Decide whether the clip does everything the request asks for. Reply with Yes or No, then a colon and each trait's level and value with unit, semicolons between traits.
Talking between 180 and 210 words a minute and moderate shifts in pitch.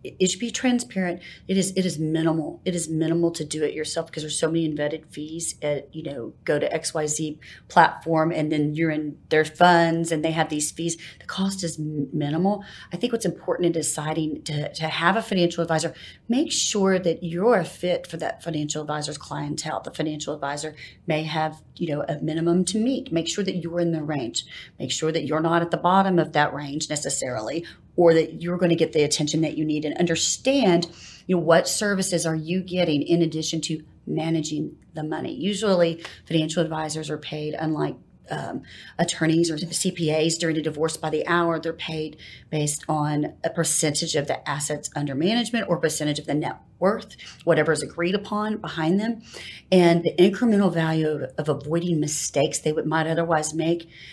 No: average, 195 wpm; narrow, 2.0 semitones